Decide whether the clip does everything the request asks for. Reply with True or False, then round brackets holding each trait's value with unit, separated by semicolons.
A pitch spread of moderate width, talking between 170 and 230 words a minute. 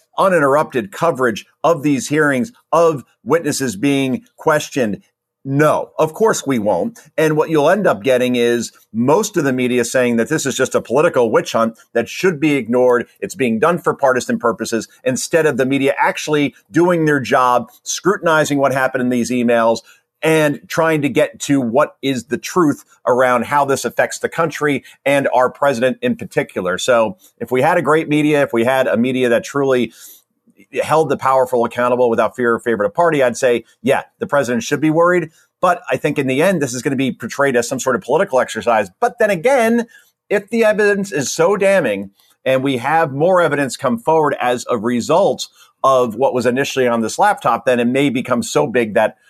True (4.0 semitones; 195 wpm)